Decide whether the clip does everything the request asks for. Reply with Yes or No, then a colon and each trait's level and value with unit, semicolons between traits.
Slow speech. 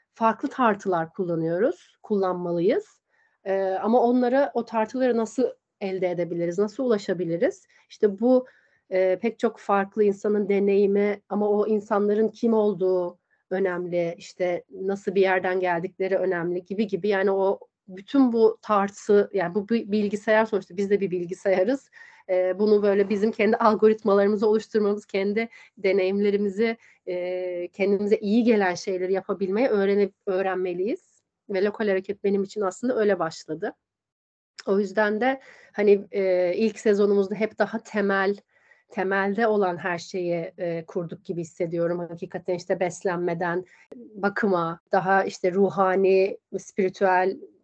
No: average, 125 wpm